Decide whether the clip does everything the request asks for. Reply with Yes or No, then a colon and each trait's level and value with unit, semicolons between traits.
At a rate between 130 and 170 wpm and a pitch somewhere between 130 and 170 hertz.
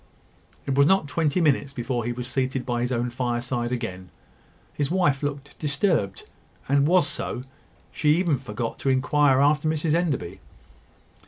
Yes: average, 155 wpm; medium, 140 Hz